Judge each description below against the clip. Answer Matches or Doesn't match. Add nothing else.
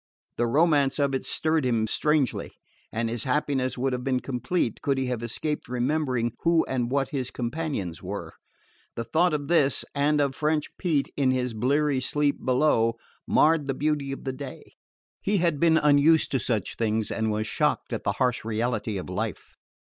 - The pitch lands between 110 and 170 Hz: Matches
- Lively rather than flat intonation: Doesn't match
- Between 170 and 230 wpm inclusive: Matches